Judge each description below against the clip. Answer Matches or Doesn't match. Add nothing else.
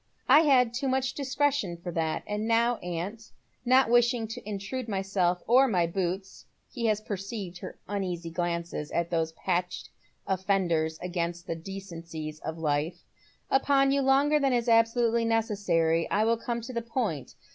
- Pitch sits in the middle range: Doesn't match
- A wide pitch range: Matches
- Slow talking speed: Doesn't match